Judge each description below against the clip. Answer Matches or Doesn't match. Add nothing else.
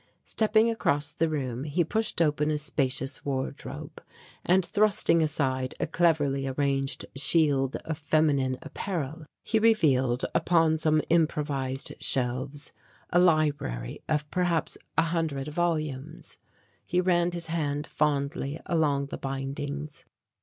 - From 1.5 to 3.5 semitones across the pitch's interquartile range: Matches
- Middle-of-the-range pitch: Matches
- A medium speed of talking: Doesn't match